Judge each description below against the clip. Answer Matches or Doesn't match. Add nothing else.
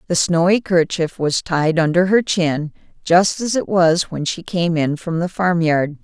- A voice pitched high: Doesn't match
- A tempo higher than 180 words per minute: Matches